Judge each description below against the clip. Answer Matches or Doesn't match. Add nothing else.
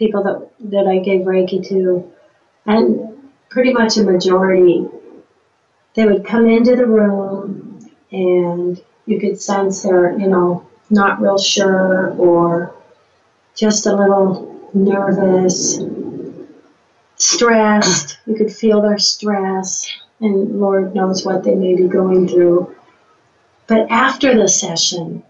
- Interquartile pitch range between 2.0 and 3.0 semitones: Matches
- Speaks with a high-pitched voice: Matches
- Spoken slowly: Matches